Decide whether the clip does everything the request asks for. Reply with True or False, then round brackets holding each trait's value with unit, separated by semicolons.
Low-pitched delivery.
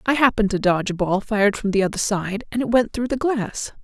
False (215 Hz)